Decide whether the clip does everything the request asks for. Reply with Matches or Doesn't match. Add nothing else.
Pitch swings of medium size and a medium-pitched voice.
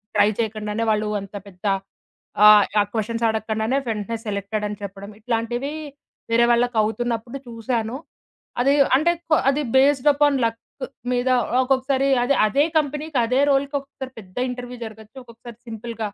Doesn't match